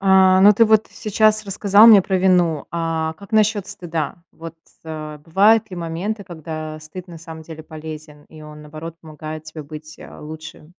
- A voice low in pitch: No, medium, 165 Hz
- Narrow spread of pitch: No, average, 3.7 semitones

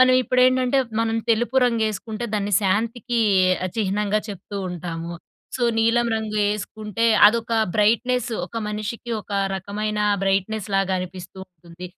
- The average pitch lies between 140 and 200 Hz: No, high, 215 Hz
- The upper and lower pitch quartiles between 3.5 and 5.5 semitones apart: No, average, 3.1 semitones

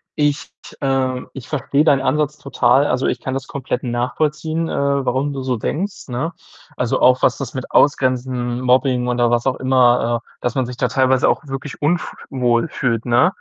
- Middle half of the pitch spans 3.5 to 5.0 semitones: No, narrow, 2.4 semitones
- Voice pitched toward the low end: Yes, low, 130 Hz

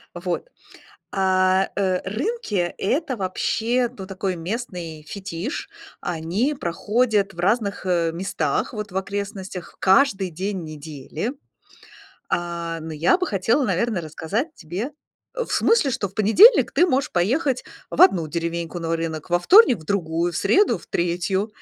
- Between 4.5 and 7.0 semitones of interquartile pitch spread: Yes, average, 5.1 semitones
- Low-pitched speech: No, high, 190 Hz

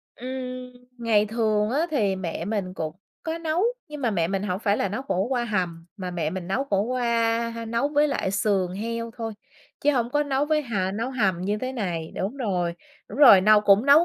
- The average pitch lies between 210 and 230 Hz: Yes, high, 220 Hz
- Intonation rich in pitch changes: No, average, 5.0 semitones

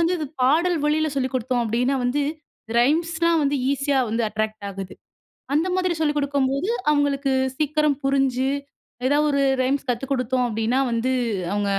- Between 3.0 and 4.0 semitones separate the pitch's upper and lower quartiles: Yes, average, 3.3 semitones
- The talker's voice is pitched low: No, very high, 275 Hz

